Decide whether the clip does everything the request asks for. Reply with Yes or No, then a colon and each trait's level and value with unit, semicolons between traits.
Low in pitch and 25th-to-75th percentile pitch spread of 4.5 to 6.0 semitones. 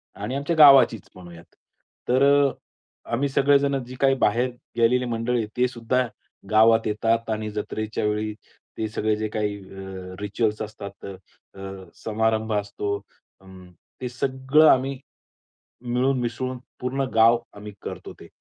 No: low, 115 Hz; average, 3.5 semitones